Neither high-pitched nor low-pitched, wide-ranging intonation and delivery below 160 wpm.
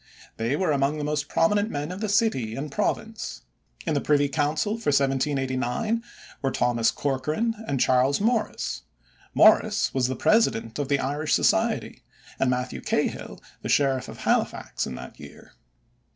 Yes: medium, 145 Hz; wide, 6.7 semitones; average, 150 wpm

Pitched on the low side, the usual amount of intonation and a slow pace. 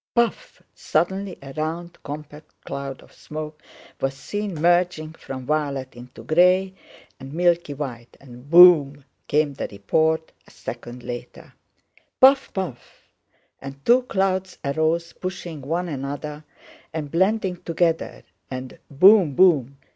No: medium, 155 Hz; average, 4.5 semitones; slow, 115 wpm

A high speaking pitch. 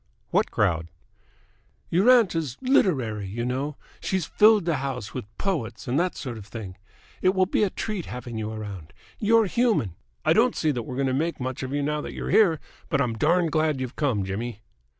No: medium, 140 Hz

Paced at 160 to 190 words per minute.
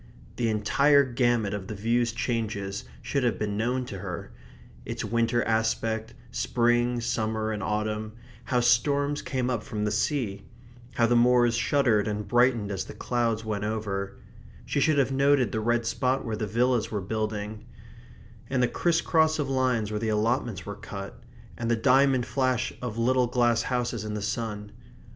Yes: average, 170 wpm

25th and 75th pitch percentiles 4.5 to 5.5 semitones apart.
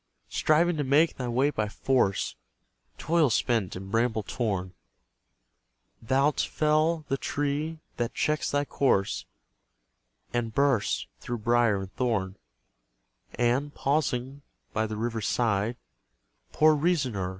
Yes: average, 4.9 semitones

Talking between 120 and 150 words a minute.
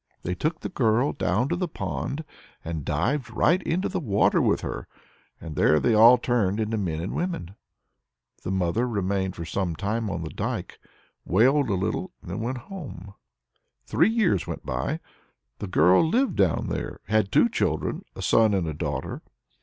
No: average, 180 wpm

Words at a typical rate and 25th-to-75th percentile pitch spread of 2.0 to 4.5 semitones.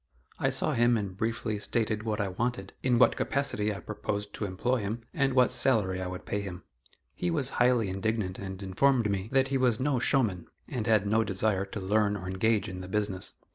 No: fast, 210 wpm; average, 3.7 semitones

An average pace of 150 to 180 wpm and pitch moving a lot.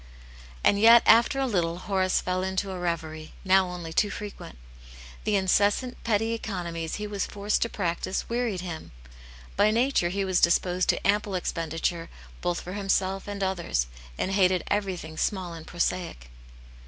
No: average, 160 wpm; average, 3.0 semitones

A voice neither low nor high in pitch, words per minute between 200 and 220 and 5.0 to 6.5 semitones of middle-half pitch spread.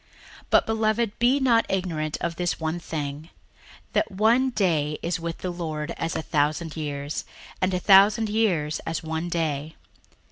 No: medium, 170 Hz; average, 165 wpm; average, 5.3 semitones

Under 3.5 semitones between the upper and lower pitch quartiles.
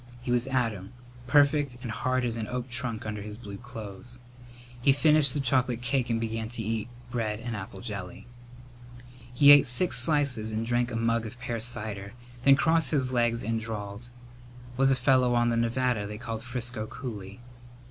Yes: narrow, 2.6 semitones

